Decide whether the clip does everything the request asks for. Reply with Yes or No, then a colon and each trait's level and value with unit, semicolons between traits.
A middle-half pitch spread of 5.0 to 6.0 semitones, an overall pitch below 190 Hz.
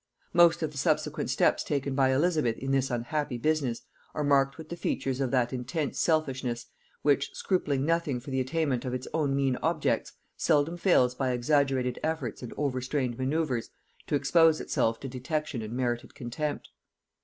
No: average, 3.3 semitones; low, 135 Hz